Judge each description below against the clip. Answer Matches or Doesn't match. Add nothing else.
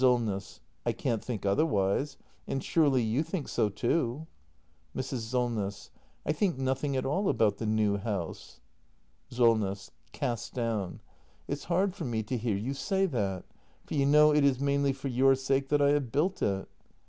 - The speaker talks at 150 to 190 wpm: Matches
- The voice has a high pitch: Doesn't match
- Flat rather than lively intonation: Doesn't match